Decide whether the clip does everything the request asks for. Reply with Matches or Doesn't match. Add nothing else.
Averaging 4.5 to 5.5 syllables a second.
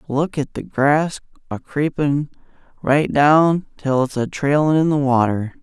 Doesn't match